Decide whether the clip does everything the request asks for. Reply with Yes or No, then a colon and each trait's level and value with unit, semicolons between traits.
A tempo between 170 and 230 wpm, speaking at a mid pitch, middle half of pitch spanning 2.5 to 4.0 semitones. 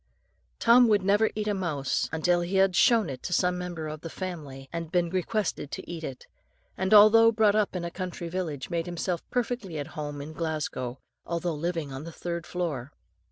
Yes: average, 200 wpm; medium, 175 Hz; average, 3.6 semitones